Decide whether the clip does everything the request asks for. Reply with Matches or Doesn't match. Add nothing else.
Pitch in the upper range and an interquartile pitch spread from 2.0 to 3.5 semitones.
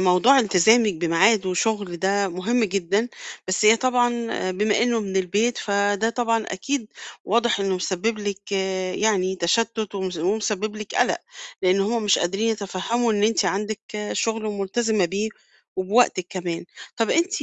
Matches